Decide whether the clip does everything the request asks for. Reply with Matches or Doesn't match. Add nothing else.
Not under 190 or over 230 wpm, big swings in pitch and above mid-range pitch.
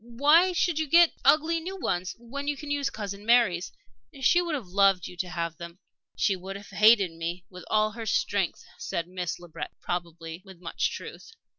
Matches